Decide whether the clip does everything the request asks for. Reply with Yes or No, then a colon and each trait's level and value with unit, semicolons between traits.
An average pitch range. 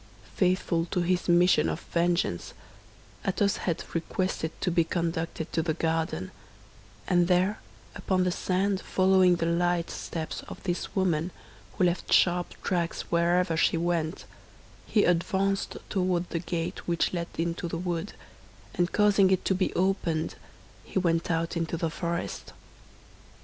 No: narrow, 1.7 semitones